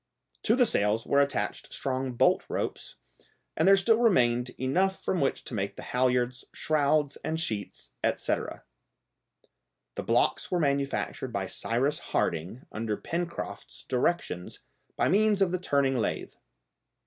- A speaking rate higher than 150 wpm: No, slow, 135 wpm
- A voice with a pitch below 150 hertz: Yes, medium, 140 Hz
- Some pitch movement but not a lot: No, wide, 6.3 semitones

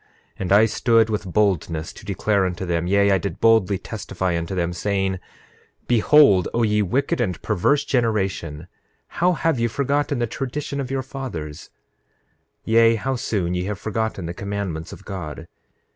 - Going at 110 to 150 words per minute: No, average, 165 wpm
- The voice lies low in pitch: Yes, low, 100 Hz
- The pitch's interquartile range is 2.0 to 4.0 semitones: No, average, 4.4 semitones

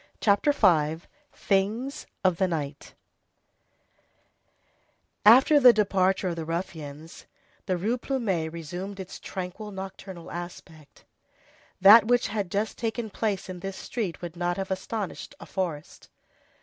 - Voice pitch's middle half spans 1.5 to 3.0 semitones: No, average, 3.7 semitones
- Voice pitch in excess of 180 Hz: Yes, high, 190 Hz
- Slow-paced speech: Yes, slow, 125 wpm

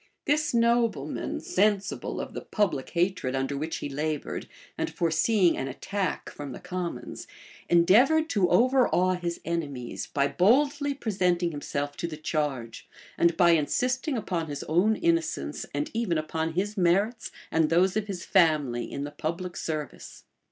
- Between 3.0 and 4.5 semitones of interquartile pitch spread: No, average, 5.2 semitones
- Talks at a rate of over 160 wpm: No, average, 150 wpm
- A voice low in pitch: No, medium, 170 Hz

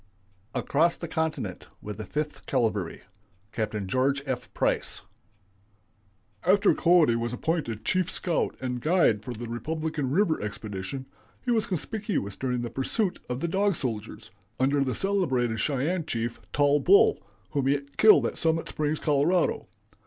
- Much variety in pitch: Yes, wide, 6.0 semitones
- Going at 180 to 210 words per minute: No, average, 145 wpm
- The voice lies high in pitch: No, medium, 140 Hz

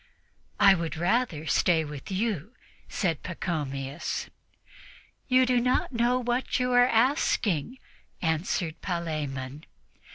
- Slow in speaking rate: Yes, slow, 105 wpm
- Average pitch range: No, wide, 7.7 semitones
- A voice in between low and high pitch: Yes, medium, 180 Hz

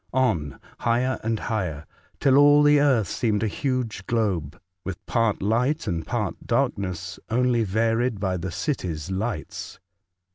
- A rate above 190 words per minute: No, average, 145 wpm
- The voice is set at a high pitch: No, low, 110 Hz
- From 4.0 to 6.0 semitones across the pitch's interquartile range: Yes, average, 5.0 semitones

